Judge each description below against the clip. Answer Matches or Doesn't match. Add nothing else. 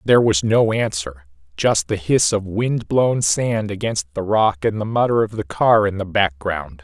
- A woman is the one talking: Doesn't match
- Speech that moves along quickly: Doesn't match